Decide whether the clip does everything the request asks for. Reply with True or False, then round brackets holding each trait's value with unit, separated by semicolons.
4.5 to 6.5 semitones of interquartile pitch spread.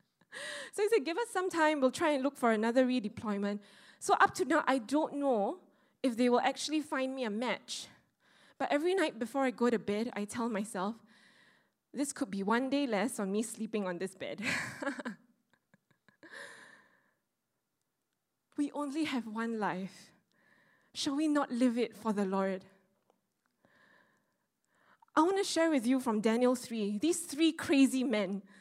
True (5.4 semitones)